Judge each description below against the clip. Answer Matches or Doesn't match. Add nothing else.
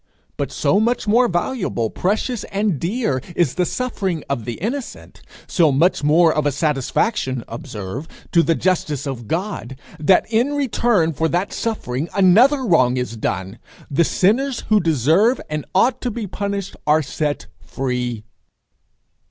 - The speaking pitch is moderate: Matches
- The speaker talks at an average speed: Matches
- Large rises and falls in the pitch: Matches